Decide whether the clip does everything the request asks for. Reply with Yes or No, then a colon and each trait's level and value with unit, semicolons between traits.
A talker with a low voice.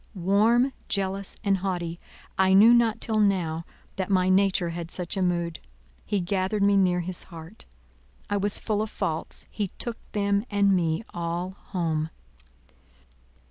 No: high, 190 Hz